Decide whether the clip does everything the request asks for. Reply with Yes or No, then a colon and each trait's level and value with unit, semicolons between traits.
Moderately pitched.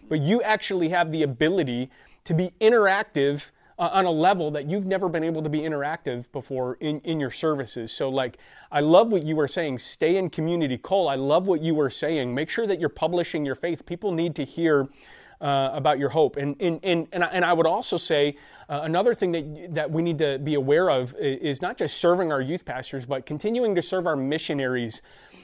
Yes: medium, 155 Hz